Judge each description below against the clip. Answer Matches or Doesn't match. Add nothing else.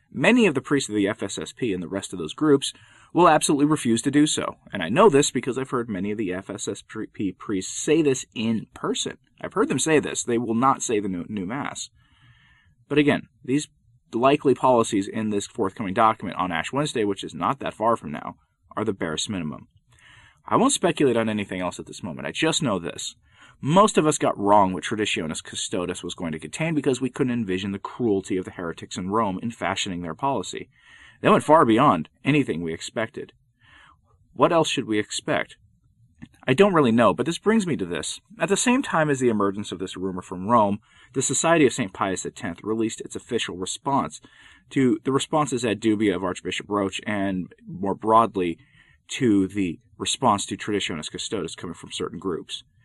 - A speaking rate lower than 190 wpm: Doesn't match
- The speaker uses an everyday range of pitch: Doesn't match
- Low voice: Matches